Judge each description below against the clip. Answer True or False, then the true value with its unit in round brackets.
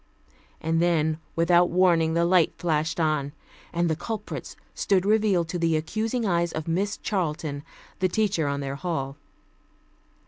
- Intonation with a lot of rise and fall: False (2.8 semitones)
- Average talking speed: True (145 wpm)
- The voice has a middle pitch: True (170 Hz)